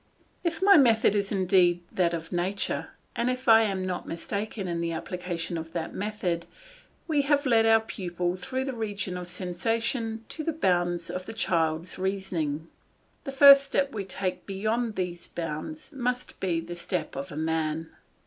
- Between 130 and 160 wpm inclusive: No, average, 170 wpm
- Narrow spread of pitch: No, average, 4.8 semitones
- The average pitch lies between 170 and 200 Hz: Yes, high, 190 Hz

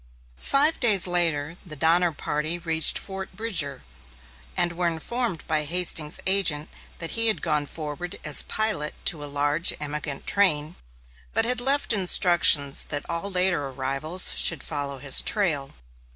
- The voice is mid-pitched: Yes, medium, 165 Hz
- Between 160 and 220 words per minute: No, average, 145 wpm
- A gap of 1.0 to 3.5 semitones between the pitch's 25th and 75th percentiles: No, average, 4.3 semitones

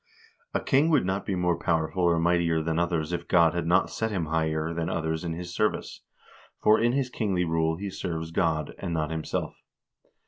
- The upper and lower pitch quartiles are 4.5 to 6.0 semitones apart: No, narrow, 2.5 semitones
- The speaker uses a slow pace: No, average, 200 wpm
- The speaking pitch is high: No, very low, 85 Hz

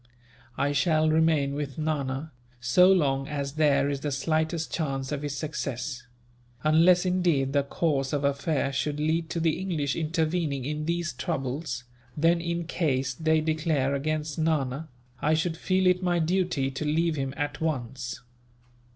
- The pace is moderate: Yes, average, 155 wpm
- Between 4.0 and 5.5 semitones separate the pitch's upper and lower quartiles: No, average, 2.9 semitones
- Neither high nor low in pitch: Yes, medium, 155 Hz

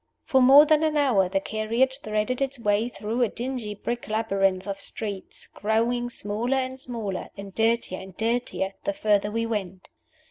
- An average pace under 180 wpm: Yes, average, 170 wpm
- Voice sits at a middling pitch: No, high, 225 Hz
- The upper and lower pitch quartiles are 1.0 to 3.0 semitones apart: No, average, 3.4 semitones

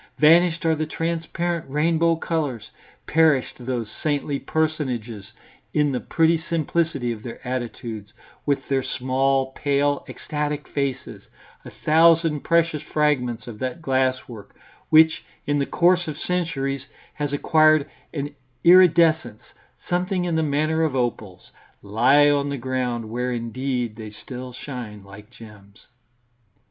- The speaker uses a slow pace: Yes, slow, 130 wpm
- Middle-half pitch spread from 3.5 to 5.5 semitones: Yes, average, 4.4 semitones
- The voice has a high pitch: No, medium, 140 Hz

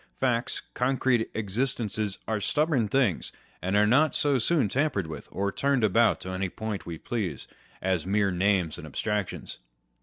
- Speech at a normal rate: Yes, average, 155 wpm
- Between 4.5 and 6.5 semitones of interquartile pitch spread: Yes, average, 4.9 semitones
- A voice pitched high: No, low, 105 Hz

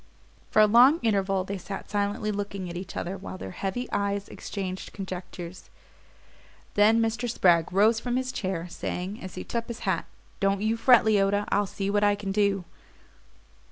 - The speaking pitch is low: No, high, 200 Hz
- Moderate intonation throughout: No, narrow, 2.3 semitones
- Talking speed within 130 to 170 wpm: No, average, 180 wpm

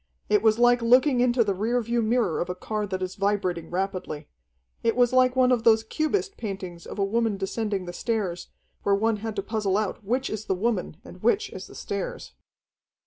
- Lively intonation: No, average, 3.8 semitones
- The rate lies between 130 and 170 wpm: No, fast, 205 wpm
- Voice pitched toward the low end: No, high, 215 Hz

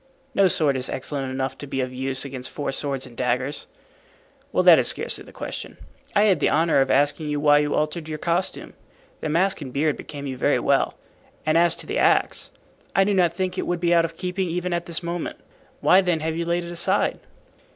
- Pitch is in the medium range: Yes, medium, 160 Hz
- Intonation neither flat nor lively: Yes, average, 3.9 semitones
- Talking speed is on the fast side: Yes, fast, 225 wpm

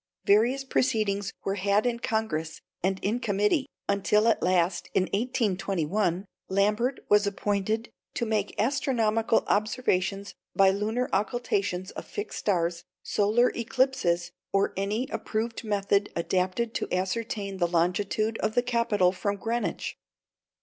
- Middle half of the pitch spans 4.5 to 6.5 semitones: No, average, 3.1 semitones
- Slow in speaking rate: Yes, slow, 125 wpm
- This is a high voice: Yes, high, 205 Hz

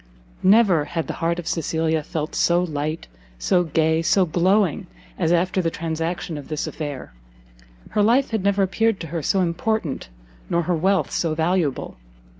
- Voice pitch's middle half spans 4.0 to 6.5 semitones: No, average, 2.9 semitones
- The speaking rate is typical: Yes, average, 165 wpm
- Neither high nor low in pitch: Yes, medium, 170 Hz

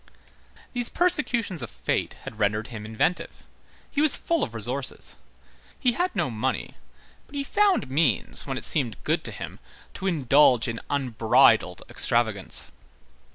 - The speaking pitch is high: No, low, 130 Hz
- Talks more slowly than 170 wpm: Yes, average, 145 wpm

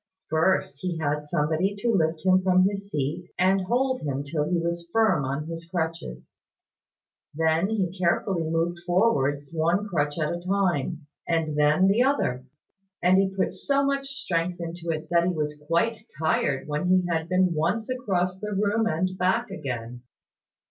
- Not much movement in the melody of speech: No, average, 3.6 semitones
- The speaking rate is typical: Yes, average, 170 wpm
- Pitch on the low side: No, medium, 175 Hz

